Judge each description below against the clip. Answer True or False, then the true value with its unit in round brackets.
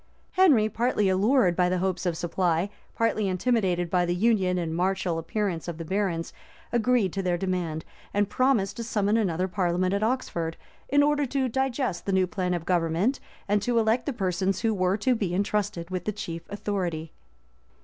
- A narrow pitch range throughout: False (3.9 semitones)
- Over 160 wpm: True (180 wpm)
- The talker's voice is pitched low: False (190 Hz)